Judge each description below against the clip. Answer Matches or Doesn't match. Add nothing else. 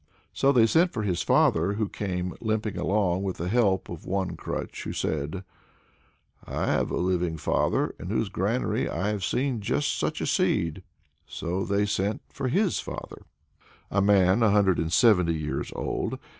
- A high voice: Doesn't match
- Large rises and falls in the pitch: Doesn't match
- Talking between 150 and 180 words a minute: Matches